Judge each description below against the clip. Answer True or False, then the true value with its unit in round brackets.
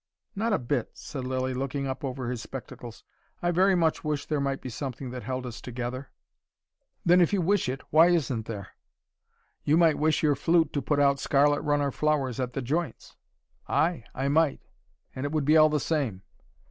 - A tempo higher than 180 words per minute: True (195 wpm)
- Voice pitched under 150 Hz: True (140 Hz)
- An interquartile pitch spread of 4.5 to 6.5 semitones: False (3.5 semitones)